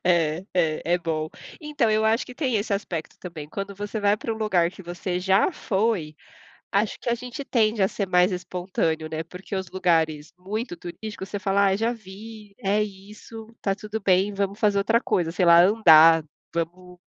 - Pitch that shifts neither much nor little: Yes, average, 3.5 semitones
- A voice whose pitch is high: Yes, high, 195 Hz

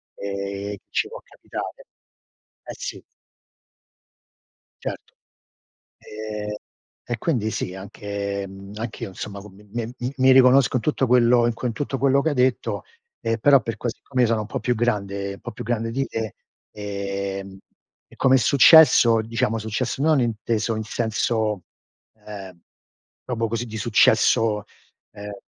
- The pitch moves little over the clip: No, average, 3.4 semitones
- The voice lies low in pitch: Yes, low, 115 Hz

